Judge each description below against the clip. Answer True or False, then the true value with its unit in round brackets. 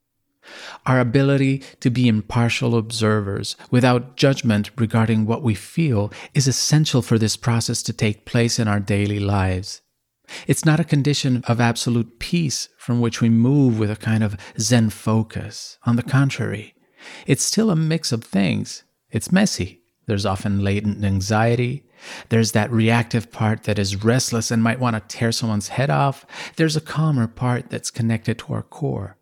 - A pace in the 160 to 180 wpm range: True (165 wpm)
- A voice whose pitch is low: True (115 Hz)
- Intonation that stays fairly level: False (3.4 semitones)